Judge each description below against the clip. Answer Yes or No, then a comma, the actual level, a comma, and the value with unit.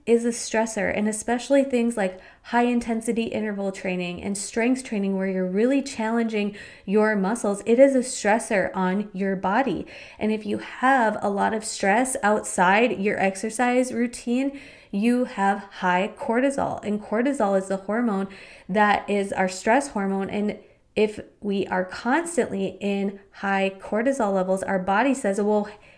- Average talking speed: Yes, average, 150 wpm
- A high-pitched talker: Yes, high, 210 Hz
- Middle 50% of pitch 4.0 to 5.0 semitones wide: No, average, 3.5 semitones